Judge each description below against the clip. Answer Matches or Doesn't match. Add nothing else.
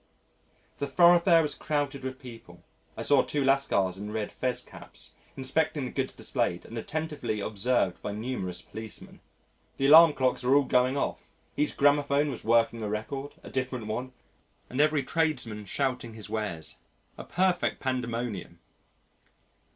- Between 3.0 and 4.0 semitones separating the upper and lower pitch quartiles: Doesn't match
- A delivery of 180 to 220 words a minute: Doesn't match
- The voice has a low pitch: Matches